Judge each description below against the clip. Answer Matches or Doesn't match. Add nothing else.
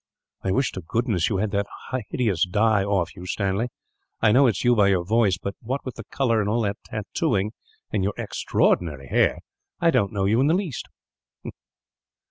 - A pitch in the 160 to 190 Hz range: Doesn't match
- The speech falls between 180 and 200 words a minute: Matches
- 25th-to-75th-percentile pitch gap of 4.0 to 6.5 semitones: Doesn't match